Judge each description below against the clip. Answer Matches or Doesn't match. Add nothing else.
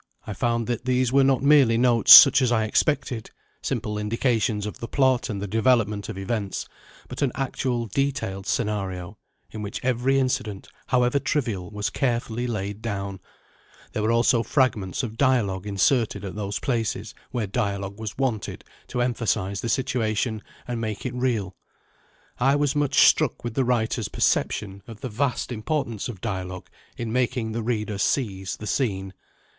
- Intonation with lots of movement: Doesn't match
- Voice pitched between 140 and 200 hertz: Doesn't match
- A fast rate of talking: Doesn't match